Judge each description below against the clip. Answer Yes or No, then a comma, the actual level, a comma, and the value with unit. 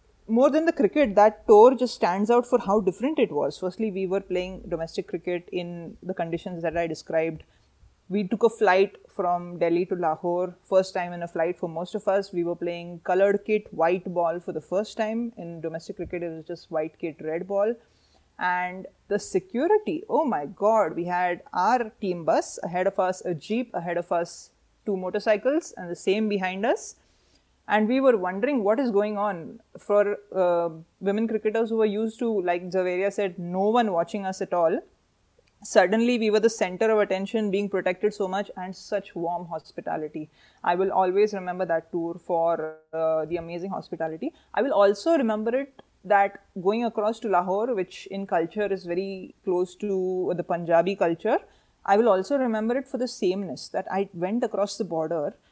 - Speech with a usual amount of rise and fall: Yes, average, 3.6 semitones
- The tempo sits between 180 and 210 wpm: Yes, average, 190 wpm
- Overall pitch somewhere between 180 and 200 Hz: Yes, high, 190 Hz